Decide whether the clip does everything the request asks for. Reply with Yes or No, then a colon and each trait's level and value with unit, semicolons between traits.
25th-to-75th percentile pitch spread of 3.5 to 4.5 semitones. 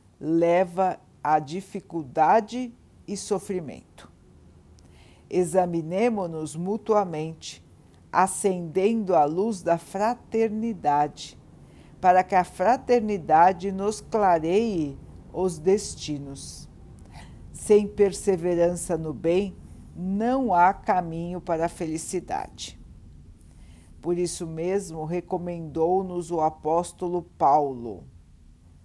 Yes: average, 3.9 semitones